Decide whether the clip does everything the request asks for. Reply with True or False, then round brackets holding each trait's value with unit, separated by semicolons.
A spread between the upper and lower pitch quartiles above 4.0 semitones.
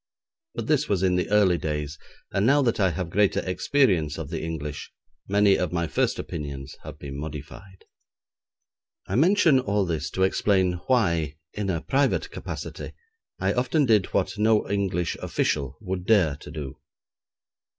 True (5.0 semitones)